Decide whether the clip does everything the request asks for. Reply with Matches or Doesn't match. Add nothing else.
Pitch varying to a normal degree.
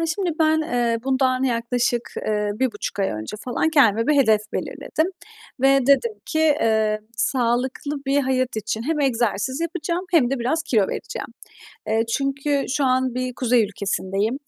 Matches